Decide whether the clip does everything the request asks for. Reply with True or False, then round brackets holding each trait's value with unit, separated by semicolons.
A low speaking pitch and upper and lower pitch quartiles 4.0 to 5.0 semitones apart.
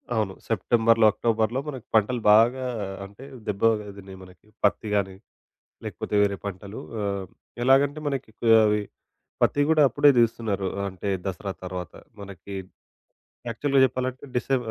True (110 Hz; 4.3 semitones)